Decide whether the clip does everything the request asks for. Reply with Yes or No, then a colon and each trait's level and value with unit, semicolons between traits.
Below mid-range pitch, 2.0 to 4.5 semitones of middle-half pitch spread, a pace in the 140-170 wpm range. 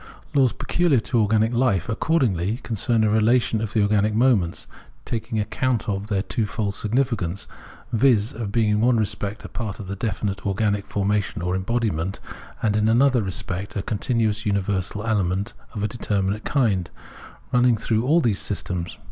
Yes: low, 105 Hz; average, 2.7 semitones; average, 165 wpm